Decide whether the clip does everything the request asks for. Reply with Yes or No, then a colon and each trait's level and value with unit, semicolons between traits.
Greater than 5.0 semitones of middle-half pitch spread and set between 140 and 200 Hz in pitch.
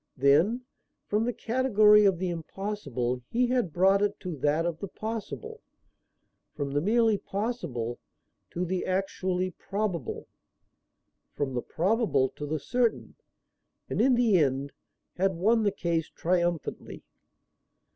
Yes: wide, 5.6 semitones; medium, 185 Hz